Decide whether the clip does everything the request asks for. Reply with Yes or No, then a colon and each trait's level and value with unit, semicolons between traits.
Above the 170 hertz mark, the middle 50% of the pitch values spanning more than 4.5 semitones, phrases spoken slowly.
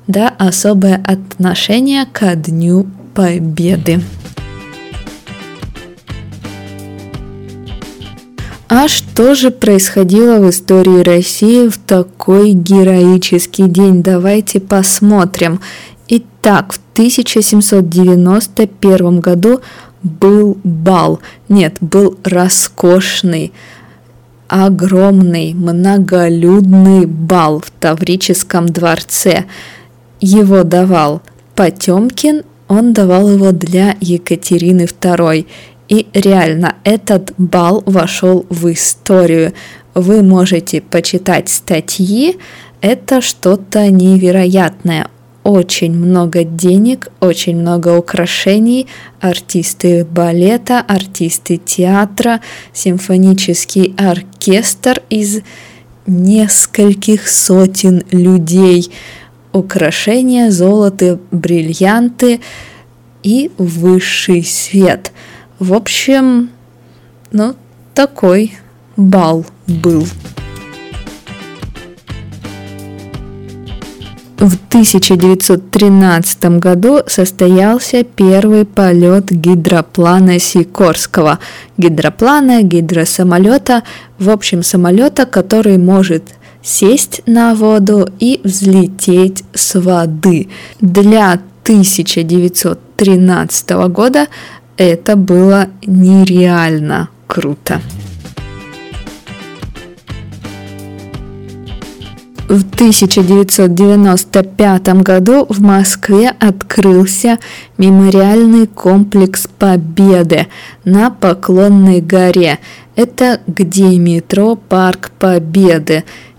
No: medium, 185 Hz; average, 2.7 semitones; slow, 70 wpm